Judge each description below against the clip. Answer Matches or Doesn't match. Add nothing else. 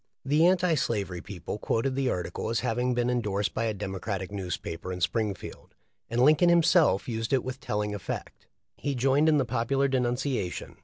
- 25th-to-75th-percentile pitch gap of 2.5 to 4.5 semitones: Doesn't match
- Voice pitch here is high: Doesn't match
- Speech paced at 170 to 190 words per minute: Matches